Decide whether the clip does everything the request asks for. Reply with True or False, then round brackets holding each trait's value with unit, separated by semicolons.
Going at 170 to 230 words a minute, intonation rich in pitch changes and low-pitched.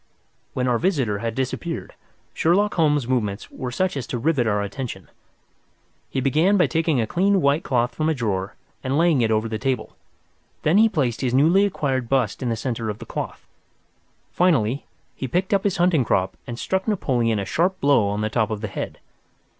True (195 wpm; 6.4 semitones; 130 Hz)